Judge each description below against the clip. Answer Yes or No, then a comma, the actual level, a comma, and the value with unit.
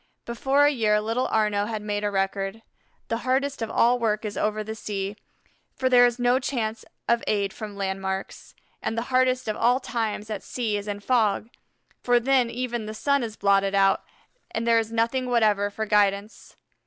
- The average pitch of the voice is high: Yes, high, 220 Hz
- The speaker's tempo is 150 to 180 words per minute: No, average, 190 wpm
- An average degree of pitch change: Yes, average, 3.0 semitones